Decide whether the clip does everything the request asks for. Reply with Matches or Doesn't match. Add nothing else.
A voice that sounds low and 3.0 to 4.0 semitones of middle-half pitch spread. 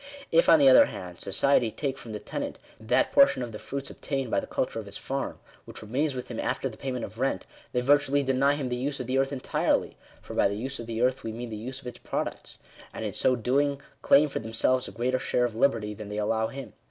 Matches